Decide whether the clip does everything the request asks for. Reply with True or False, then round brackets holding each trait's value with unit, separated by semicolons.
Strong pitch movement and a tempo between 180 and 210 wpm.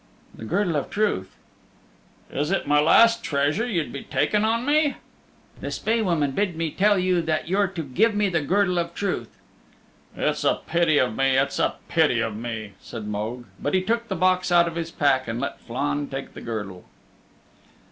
True (6.5 semitones; 190 wpm)